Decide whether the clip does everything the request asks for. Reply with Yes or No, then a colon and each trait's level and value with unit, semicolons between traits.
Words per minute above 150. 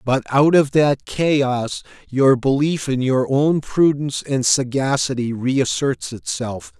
No: slow, 135 wpm